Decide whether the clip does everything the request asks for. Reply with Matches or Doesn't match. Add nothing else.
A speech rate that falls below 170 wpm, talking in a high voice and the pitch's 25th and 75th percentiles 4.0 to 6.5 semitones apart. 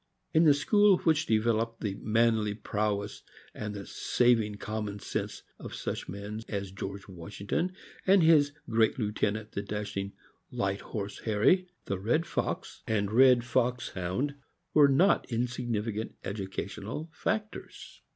Doesn't match